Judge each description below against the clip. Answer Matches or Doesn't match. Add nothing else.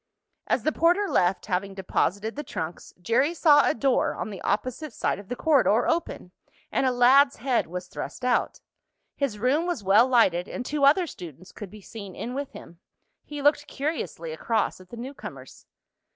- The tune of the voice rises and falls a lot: Matches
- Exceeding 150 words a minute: Matches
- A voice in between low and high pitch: Doesn't match